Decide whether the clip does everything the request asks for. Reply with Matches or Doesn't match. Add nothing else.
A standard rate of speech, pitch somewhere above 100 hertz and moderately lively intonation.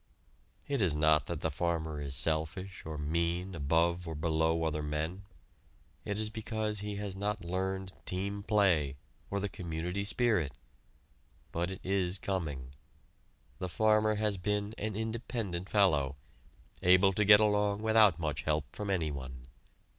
Doesn't match